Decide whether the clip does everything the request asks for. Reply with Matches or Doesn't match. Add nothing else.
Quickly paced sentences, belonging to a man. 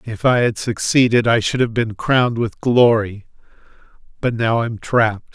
Doesn't match